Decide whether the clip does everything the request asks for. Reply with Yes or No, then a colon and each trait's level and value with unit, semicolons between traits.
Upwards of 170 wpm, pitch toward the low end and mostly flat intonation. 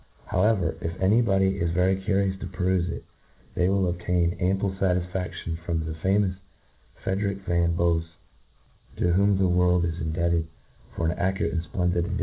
Yes: average, 180 wpm; very low, 90 Hz; narrow, 1.9 semitones